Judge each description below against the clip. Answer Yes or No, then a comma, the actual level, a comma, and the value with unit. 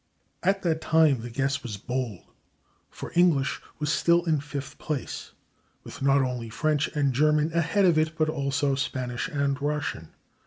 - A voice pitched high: No, medium, 145 Hz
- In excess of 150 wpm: Yes, average, 160 wpm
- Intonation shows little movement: No, average, 3.0 semitones